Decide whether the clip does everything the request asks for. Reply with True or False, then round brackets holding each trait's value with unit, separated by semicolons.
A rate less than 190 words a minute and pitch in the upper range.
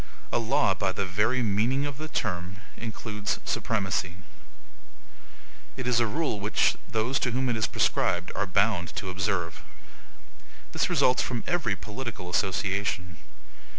False (140 wpm; 105 Hz)